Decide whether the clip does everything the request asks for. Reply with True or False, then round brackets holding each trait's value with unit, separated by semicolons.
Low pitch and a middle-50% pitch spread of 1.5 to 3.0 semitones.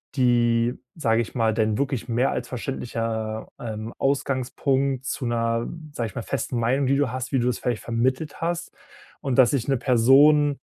True (125 Hz; 2.7 semitones)